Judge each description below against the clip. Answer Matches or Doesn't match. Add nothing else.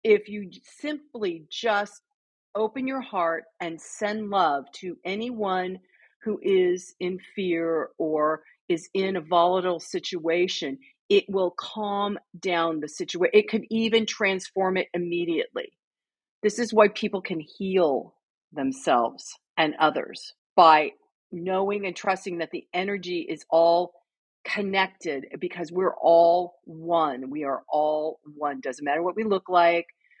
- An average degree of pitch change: Matches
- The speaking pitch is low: Doesn't match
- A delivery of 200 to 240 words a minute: Doesn't match